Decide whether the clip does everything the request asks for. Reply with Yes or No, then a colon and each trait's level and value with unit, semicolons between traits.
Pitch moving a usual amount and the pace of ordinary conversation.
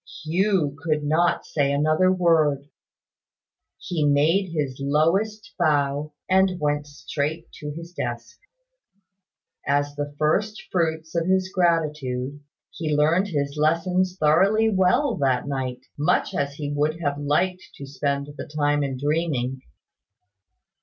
No: average, 3.3 semitones; slow, 125 wpm